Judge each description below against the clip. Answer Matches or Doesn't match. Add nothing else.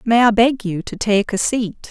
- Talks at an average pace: Doesn't match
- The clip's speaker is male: Doesn't match